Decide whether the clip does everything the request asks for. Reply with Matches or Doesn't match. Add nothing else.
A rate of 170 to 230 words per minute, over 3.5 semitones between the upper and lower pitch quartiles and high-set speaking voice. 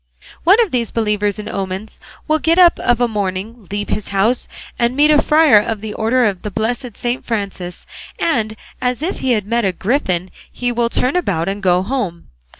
Matches